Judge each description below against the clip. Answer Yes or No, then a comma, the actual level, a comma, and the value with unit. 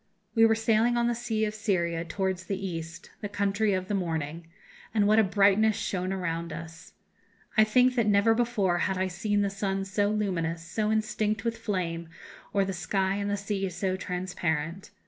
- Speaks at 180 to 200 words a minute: Yes, average, 185 wpm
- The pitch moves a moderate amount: Yes, average, 3.2 semitones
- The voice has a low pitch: No, high, 195 Hz